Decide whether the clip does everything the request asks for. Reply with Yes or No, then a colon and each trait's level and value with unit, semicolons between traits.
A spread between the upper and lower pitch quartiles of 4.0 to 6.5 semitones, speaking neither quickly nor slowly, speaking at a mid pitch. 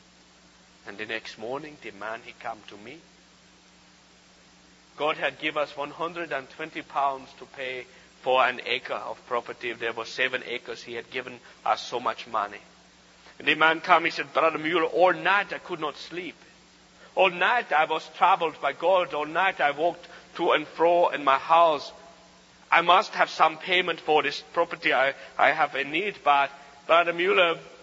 No: average, 3.5 semitones; average, 175 wpm; medium, 155 Hz